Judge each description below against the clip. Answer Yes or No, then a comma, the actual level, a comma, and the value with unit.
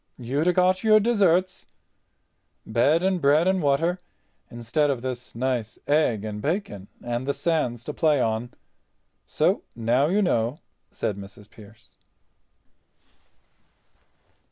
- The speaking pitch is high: No, medium, 140 Hz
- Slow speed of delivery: Yes, slow, 120 wpm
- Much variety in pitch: Yes, wide, 6.8 semitones